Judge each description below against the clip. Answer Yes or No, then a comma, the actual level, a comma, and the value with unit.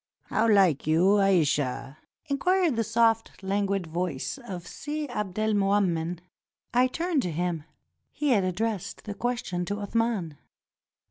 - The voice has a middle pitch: No, high, 200 Hz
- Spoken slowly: Yes, slow, 125 wpm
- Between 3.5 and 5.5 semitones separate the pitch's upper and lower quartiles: Yes, average, 4.6 semitones